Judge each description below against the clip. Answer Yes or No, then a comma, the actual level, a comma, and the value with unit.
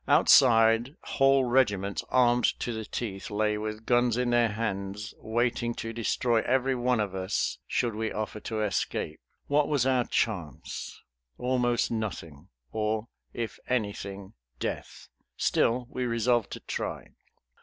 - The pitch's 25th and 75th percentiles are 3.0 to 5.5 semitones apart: No, narrow, 2.5 semitones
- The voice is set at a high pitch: No, low, 115 Hz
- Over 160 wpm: No, slow, 135 wpm